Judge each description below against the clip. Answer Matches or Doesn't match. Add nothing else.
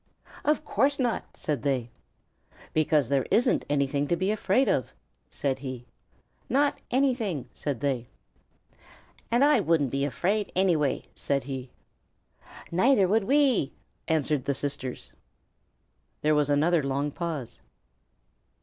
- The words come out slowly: Matches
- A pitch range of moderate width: Doesn't match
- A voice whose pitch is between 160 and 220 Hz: Doesn't match